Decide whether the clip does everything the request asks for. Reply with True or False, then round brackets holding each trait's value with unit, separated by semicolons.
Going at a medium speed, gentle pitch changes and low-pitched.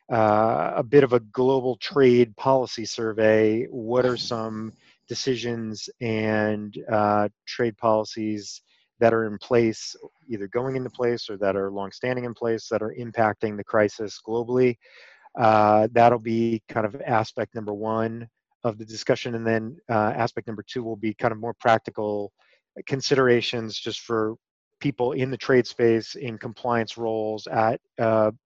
True (155 wpm; 2.0 semitones; 115 Hz)